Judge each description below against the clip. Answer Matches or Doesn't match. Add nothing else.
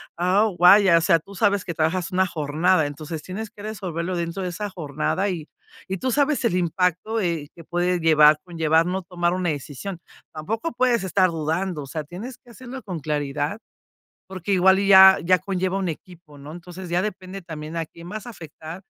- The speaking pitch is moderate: Matches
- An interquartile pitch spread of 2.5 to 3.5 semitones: Matches